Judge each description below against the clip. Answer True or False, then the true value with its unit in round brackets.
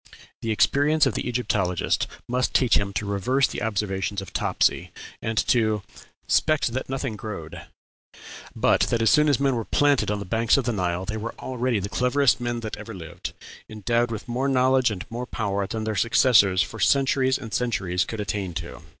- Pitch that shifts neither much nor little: True (4.0 semitones)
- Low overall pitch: True (115 Hz)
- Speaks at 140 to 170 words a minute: False (190 wpm)